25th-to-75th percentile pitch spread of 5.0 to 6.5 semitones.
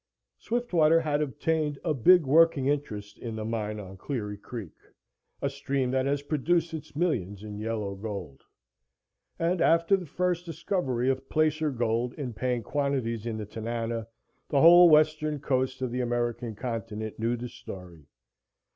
Yes: wide, 5.5 semitones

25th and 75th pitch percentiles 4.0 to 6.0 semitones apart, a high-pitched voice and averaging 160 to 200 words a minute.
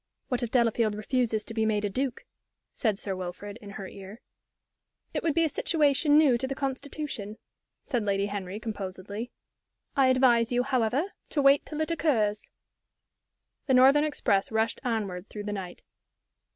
Yes: average, 4.8 semitones; high, 230 Hz; average, 165 wpm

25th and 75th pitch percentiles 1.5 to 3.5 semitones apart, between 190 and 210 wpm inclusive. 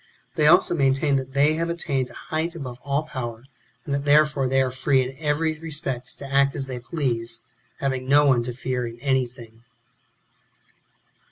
No: average, 2.8 semitones; average, 180 wpm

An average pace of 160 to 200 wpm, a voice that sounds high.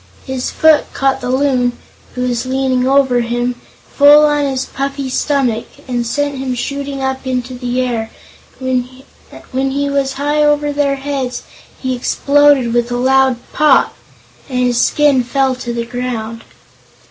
No: average, 150 wpm; very high, 260 Hz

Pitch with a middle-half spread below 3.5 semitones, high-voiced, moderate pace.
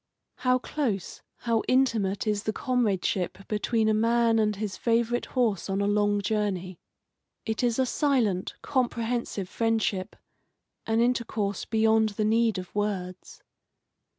No: average, 2.7 semitones; high, 220 Hz; slow, 130 wpm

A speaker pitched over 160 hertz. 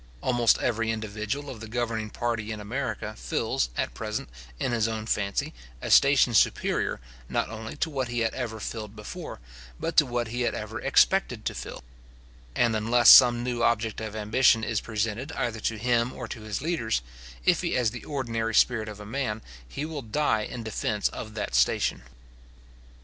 No: low, 115 Hz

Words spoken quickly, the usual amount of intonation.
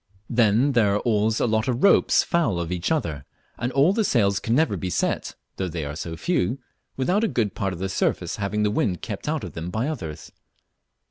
No: fast, 220 wpm; wide, 6.2 semitones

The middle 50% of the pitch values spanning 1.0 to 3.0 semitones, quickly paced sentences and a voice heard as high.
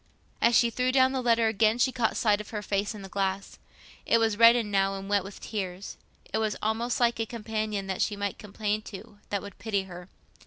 Yes: narrow, 2.5 semitones; fast, 220 wpm; high, 210 Hz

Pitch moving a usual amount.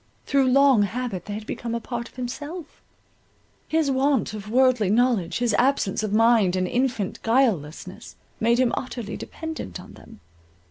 Yes: average, 3.9 semitones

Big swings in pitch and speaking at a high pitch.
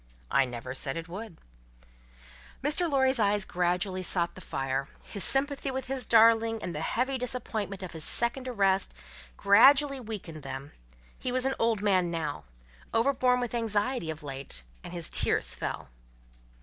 Yes: wide, 6.9 semitones; high, 205 Hz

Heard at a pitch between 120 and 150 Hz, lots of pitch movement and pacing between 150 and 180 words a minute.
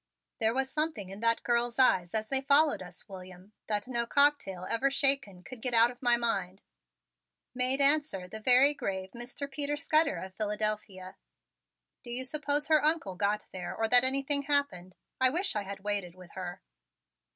No: high, 235 Hz; wide, 6.1 semitones; average, 175 wpm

